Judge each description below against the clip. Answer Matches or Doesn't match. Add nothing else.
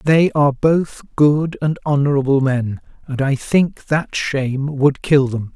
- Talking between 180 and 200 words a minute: Doesn't match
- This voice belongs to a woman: Doesn't match